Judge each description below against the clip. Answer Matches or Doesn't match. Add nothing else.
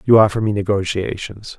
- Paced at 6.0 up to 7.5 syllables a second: Doesn't match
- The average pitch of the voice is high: Doesn't match